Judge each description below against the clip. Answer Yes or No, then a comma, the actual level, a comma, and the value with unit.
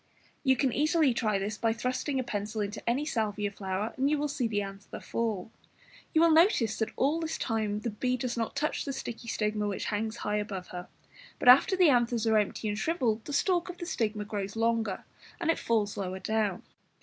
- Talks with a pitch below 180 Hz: No, high, 225 Hz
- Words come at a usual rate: No, fast, 210 wpm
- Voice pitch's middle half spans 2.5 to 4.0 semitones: No, average, 4.4 semitones